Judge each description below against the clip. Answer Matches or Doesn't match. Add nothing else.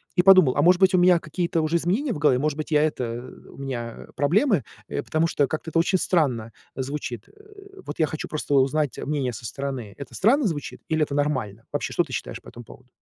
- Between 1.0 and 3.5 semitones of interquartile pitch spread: Doesn't match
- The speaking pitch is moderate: Matches